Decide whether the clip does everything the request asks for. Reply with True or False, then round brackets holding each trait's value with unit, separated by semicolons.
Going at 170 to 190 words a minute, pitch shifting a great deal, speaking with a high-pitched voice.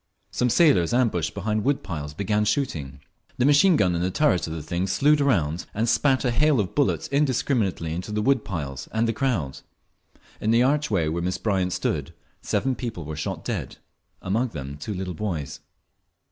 False (185 wpm; 7.2 semitones; 105 Hz)